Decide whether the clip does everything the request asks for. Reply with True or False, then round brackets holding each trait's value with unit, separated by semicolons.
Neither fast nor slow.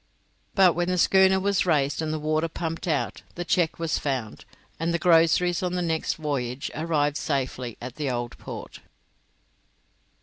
True (165 wpm)